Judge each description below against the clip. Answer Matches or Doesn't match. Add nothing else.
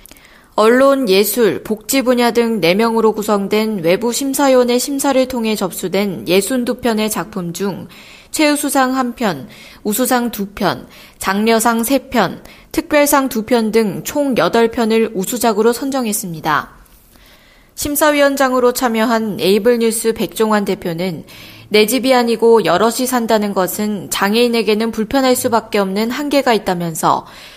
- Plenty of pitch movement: Doesn't match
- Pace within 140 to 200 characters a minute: Doesn't match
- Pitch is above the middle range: Matches